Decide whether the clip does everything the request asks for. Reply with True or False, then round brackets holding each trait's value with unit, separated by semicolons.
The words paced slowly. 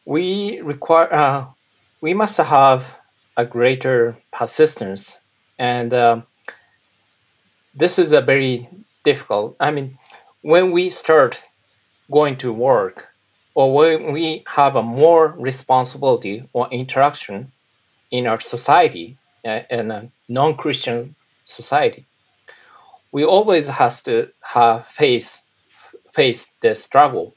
True (105 wpm)